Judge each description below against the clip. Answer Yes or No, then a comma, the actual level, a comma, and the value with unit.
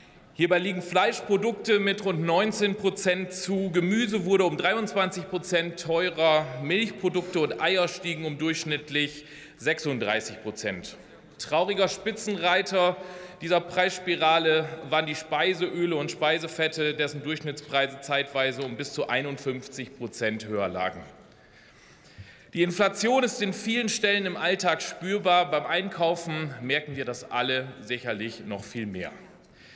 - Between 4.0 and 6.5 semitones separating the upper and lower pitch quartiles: Yes, average, 4.3 semitones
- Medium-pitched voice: Yes, medium, 165 Hz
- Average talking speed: No, slow, 120 wpm